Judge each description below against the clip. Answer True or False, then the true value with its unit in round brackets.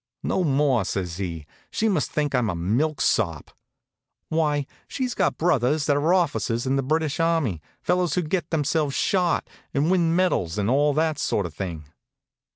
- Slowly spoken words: False (165 wpm)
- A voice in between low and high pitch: True (145 Hz)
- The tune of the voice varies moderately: False (6.4 semitones)